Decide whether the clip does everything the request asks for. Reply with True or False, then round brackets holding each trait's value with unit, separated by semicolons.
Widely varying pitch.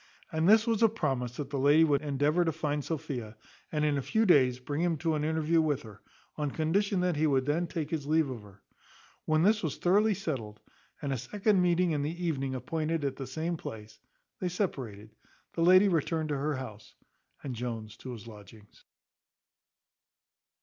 False (4.4 semitones)